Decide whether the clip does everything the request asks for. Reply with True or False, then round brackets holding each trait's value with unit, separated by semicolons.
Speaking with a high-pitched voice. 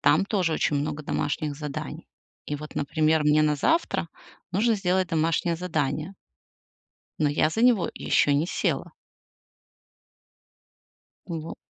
False (155 Hz)